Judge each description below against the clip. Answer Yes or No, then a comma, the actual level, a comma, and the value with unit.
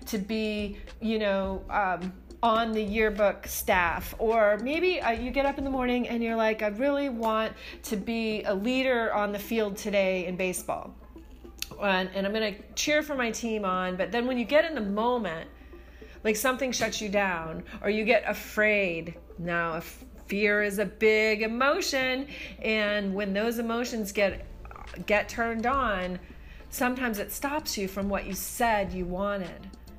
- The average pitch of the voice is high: Yes, high, 215 Hz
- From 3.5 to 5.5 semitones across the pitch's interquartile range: No, average, 2.9 semitones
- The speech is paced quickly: No, average, 170 wpm